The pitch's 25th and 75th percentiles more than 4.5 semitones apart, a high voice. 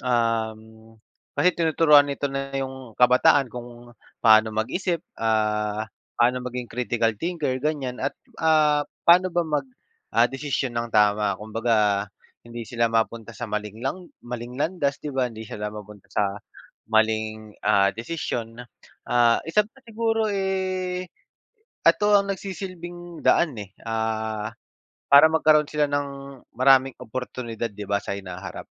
No: wide, 5.4 semitones; low, 125 Hz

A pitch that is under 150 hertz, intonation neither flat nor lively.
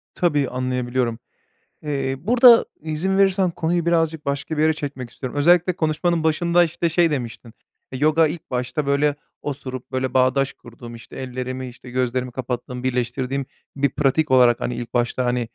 Yes: low, 135 Hz; average, 4.0 semitones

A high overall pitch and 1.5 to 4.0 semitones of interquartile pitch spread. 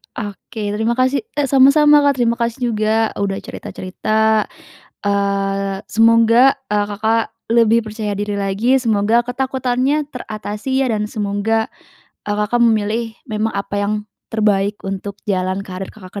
Yes: high, 220 Hz; average, 2.7 semitones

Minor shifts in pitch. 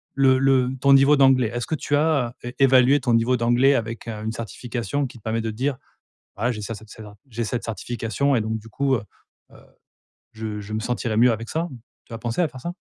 No: average, 3.2 semitones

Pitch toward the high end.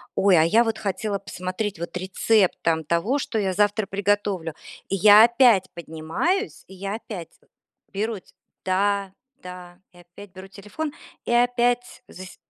Yes: high, 200 Hz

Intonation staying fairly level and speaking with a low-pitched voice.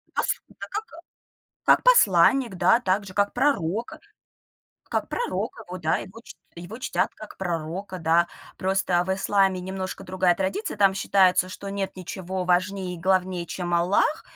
No: narrow, 1.9 semitones; high, 190 Hz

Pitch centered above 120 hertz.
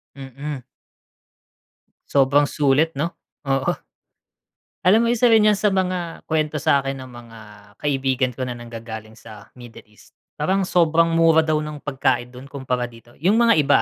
Yes: medium, 140 Hz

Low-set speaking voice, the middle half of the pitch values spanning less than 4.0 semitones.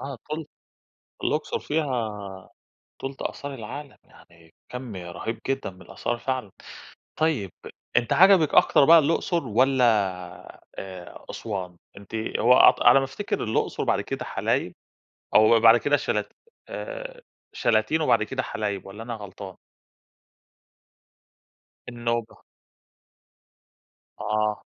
No: low, 120 Hz; average, 5.0 semitones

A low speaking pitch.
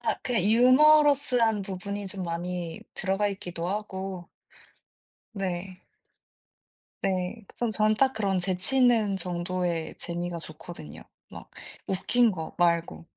No: high, 190 Hz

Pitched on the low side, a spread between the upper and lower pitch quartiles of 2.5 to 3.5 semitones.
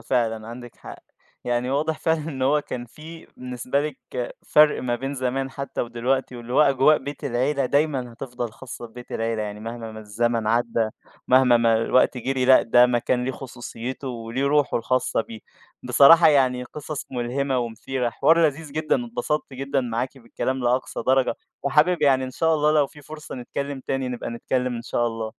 Yes: low, 130 Hz; average, 2.8 semitones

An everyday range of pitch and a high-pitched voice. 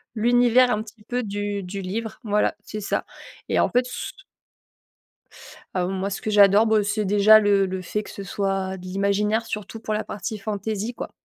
No: narrow, 1.8 semitones; high, 210 Hz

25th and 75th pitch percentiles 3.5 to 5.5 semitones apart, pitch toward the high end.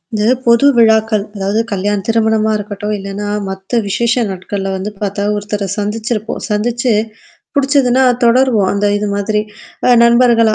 No: narrow, 2.5 semitones; high, 215 Hz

